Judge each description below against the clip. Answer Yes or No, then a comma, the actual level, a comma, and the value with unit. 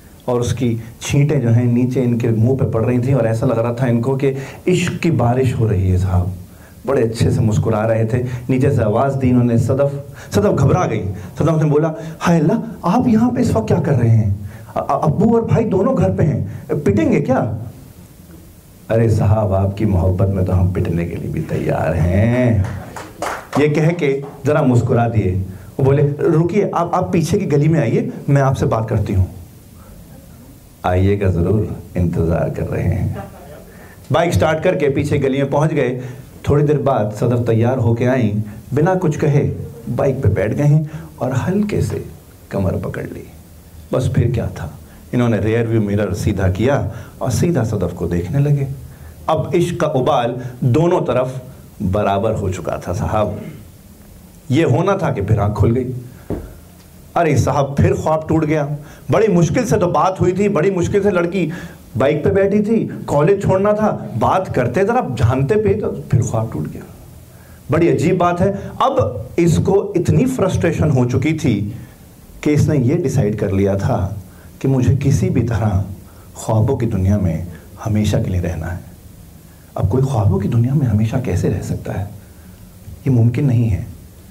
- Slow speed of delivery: No, average, 175 wpm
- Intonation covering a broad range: Yes, wide, 6.4 semitones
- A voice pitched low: Yes, low, 120 Hz